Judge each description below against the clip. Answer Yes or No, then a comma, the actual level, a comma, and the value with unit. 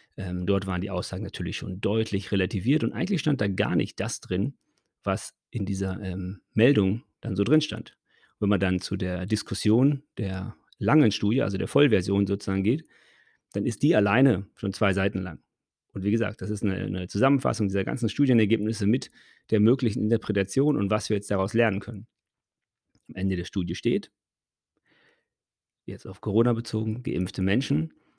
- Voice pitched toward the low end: Yes, low, 105 Hz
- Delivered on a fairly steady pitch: No, average, 3.0 semitones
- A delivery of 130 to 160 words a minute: No, average, 170 wpm